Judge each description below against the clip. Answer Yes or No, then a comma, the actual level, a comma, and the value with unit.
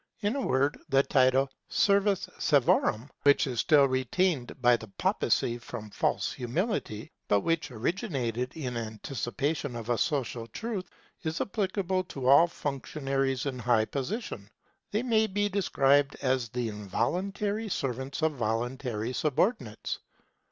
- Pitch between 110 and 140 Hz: Yes, low, 135 Hz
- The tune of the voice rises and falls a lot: Yes, wide, 6.6 semitones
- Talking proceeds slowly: Yes, slow, 130 wpm